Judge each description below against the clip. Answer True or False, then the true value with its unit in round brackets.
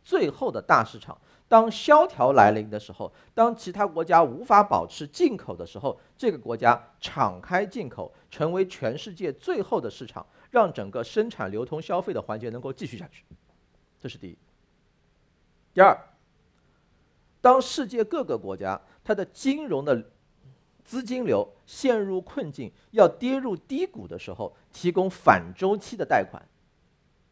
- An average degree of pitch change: False (7.8 semitones)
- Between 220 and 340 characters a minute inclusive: True (230 characters per minute)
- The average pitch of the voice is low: False (215 Hz)